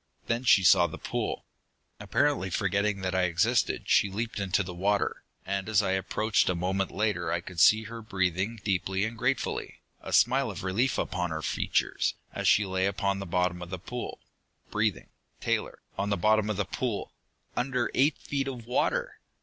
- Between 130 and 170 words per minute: No, average, 180 wpm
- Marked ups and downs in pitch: No, average, 3.2 semitones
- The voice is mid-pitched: No, low, 100 Hz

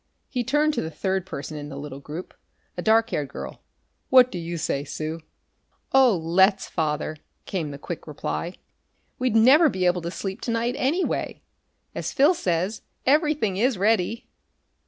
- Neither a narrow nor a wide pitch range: No, wide, 7.4 semitones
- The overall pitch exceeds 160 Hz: Yes, high, 190 Hz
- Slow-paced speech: No, average, 165 wpm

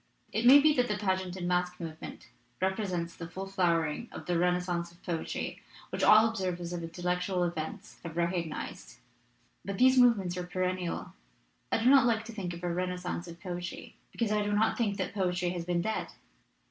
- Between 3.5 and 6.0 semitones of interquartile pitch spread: No, average, 3.0 semitones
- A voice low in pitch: No, medium, 180 Hz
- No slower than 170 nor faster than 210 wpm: Yes, average, 200 wpm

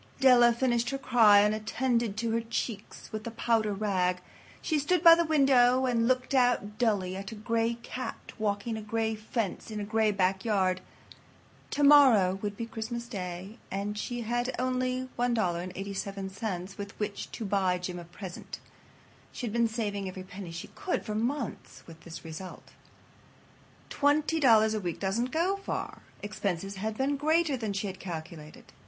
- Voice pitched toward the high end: Yes, high, 220 Hz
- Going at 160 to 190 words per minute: Yes, average, 165 wpm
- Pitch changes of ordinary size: Yes, average, 4.0 semitones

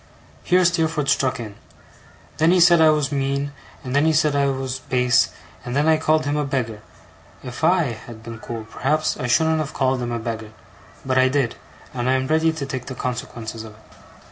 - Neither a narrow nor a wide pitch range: Yes, average, 4.1 semitones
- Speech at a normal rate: No, fast, 210 wpm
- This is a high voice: No, low, 135 Hz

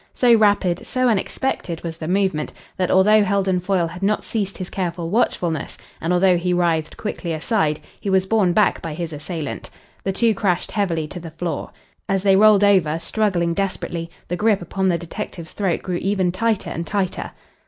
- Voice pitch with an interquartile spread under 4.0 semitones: Yes, average, 3.1 semitones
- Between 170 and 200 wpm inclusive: Yes, average, 185 wpm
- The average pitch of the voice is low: No, medium, 185 Hz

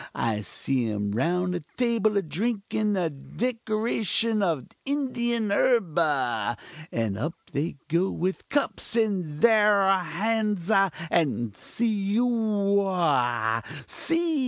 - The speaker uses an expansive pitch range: Yes, wide, 6.9 semitones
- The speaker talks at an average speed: No, slow, 115 wpm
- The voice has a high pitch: Yes, high, 195 Hz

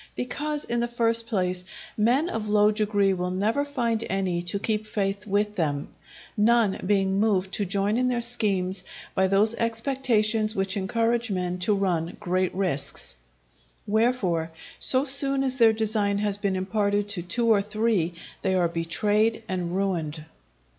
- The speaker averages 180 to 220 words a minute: No, average, 155 wpm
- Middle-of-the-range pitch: No, high, 205 Hz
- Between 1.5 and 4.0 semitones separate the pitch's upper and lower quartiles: Yes, average, 3.4 semitones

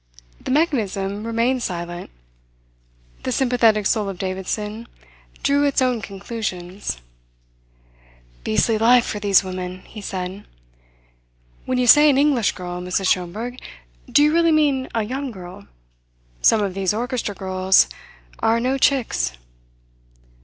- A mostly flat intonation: No, average, 5.2 semitones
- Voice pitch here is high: Yes, high, 215 Hz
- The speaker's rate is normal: No, slow, 125 wpm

